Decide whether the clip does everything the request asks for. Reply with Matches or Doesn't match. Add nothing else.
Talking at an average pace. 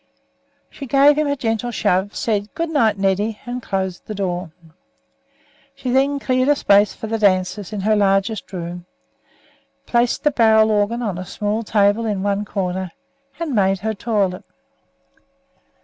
Matches